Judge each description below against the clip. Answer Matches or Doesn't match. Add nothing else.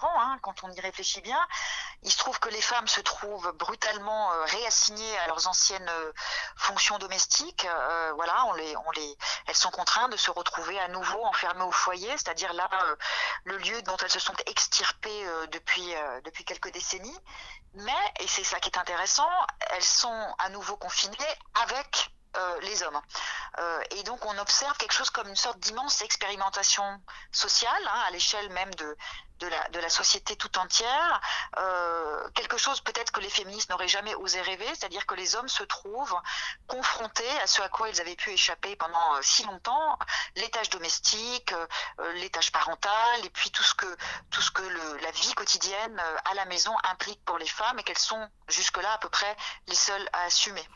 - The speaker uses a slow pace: Doesn't match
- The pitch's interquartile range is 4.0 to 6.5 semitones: Doesn't match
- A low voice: Doesn't match